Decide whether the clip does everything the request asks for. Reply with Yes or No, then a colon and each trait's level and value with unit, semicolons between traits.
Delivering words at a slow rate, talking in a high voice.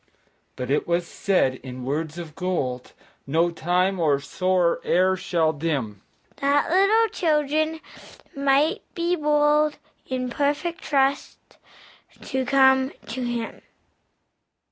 Yes: slow, 115 wpm; high, 225 Hz